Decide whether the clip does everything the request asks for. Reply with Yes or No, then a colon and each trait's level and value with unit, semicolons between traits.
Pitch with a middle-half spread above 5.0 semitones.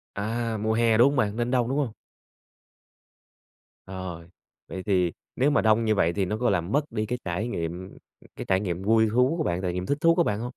No: average, 4.5 semitones